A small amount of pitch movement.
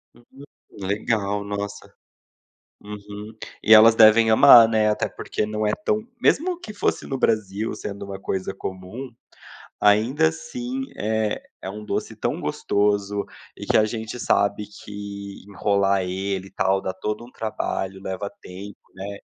Yes: narrow, 2.0 semitones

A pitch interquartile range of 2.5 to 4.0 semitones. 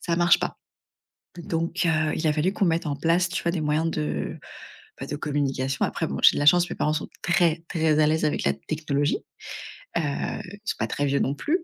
Yes: average, 2.8 semitones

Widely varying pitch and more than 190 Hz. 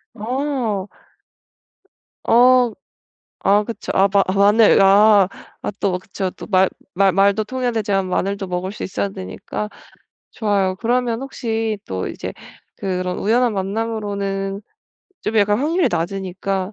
No: average, 2.7 semitones; high, 200 Hz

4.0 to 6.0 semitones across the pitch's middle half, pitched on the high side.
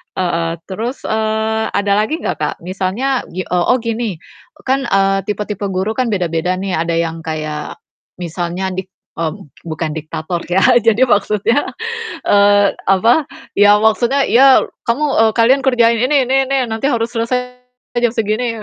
Yes: average, 4.5 semitones; high, 210 Hz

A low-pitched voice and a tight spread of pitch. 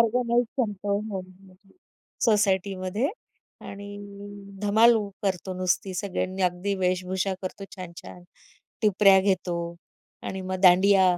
No: high, 190 Hz; narrow, 1.7 semitones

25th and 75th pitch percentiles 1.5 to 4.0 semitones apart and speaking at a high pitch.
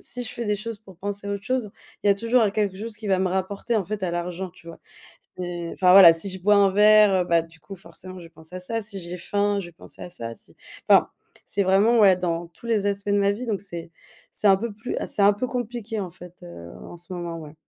Yes: average, 3.0 semitones; high, 195 Hz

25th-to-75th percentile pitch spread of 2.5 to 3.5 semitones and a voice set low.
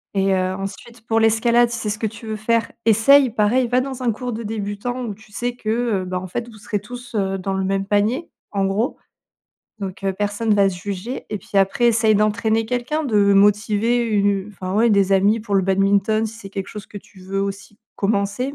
No: average, 2.9 semitones; high, 210 Hz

